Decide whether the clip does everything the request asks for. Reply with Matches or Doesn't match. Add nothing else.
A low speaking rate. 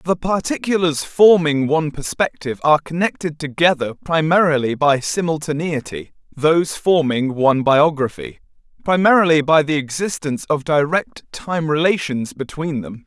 Matches